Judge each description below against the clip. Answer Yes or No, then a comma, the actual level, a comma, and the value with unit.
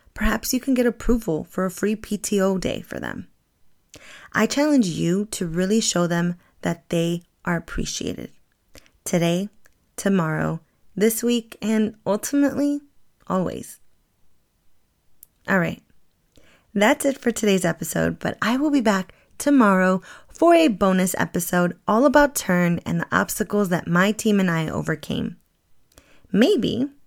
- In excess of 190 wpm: No, slow, 135 wpm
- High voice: Yes, high, 205 Hz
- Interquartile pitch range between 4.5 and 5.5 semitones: Yes, average, 5.1 semitones